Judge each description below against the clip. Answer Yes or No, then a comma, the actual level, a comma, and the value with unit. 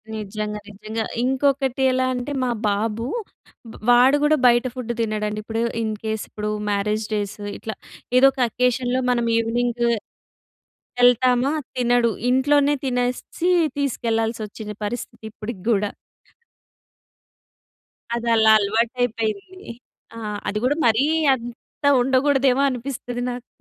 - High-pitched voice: Yes, high, 240 Hz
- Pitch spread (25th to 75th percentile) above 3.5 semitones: No, average, 2.8 semitones